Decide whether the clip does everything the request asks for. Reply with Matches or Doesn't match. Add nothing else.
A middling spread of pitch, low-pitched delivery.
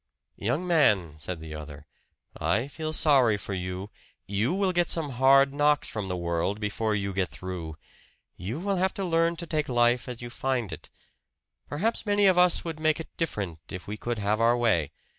Doesn't match